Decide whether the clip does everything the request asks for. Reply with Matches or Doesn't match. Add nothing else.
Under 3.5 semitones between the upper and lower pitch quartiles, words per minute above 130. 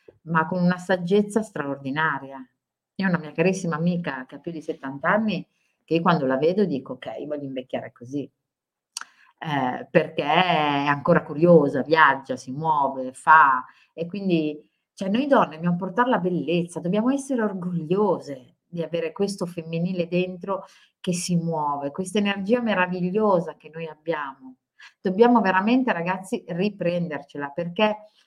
Doesn't match